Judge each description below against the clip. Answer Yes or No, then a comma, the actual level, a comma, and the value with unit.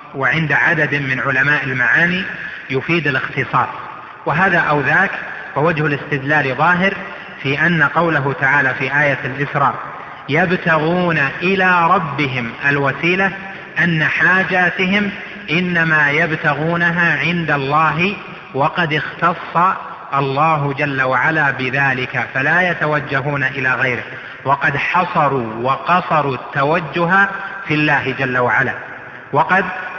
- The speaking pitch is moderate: Yes, medium, 150 Hz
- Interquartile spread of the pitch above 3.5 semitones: Yes, average, 4.3 semitones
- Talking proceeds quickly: No, average, 100 wpm